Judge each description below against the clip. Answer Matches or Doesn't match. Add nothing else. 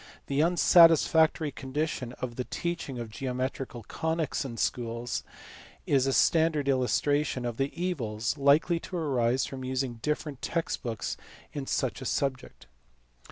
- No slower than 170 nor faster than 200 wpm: Doesn't match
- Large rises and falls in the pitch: Doesn't match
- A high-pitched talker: Doesn't match